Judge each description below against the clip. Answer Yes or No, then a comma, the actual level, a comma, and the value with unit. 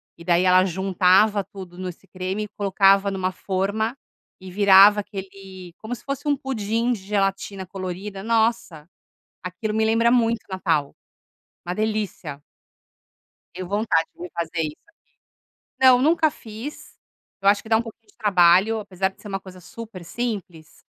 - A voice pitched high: Yes, high, 195 Hz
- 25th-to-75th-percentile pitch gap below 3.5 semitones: Yes, average, 3.1 semitones